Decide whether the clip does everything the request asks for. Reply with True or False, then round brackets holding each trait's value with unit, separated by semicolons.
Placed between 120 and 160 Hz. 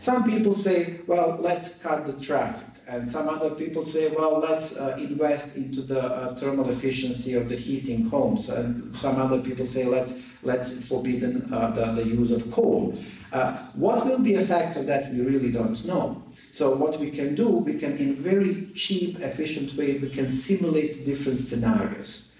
True (140 Hz)